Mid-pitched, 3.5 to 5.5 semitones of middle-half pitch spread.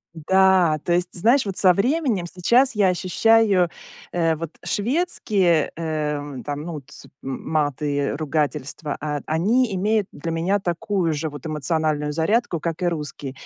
Yes: medium, 170 Hz; average, 4.6 semitones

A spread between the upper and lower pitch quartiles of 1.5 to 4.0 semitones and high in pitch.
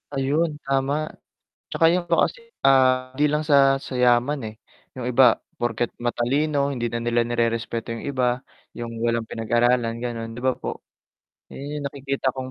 No: average, 2.9 semitones; low, 130 Hz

